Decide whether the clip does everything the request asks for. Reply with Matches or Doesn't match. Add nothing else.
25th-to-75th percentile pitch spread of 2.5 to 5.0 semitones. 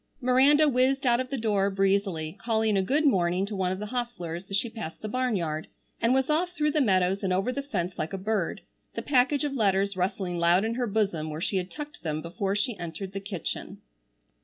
Doesn't match